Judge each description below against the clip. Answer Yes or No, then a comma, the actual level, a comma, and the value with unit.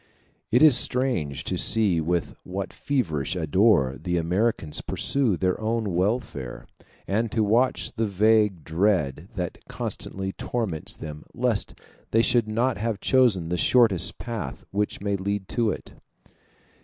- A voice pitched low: Yes, low, 100 Hz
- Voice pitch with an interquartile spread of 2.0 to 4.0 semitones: No, average, 4.7 semitones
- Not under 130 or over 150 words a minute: Yes, average, 140 wpm